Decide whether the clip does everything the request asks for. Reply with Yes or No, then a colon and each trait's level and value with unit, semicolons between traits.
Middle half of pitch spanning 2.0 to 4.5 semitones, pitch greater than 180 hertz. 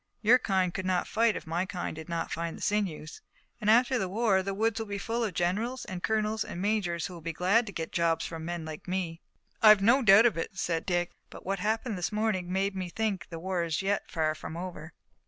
Yes: average, 3.9 semitones; high, 190 Hz